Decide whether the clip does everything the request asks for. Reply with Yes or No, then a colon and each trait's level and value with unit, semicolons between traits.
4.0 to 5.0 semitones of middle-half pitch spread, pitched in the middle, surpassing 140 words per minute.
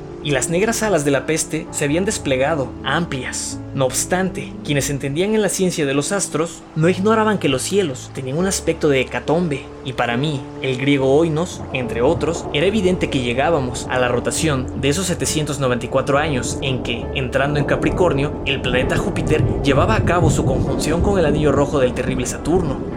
Yes: average, 4.4 semitones; medium, 150 Hz; average, 185 wpm